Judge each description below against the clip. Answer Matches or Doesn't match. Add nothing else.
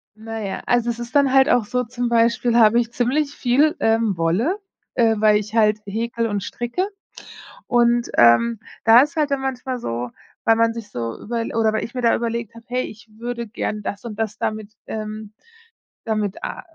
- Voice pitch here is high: Matches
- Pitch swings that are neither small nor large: Doesn't match